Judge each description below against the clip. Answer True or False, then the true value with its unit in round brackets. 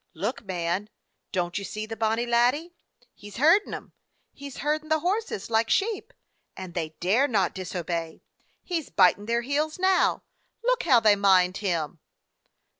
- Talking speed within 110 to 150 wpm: False (165 wpm)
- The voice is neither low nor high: False (220 Hz)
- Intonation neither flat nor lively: False (8.1 semitones)